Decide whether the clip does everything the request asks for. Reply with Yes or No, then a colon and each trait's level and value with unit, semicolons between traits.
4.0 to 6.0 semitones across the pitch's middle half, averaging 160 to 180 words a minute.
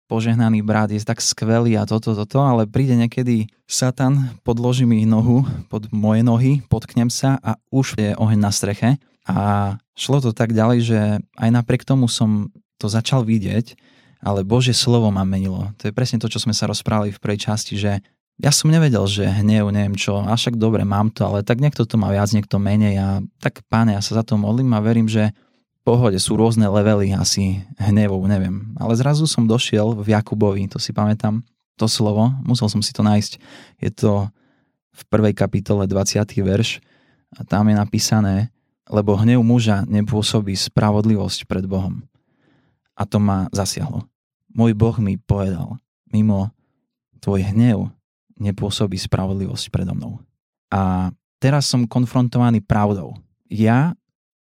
No: average, 2.8 semitones; fast, 165 wpm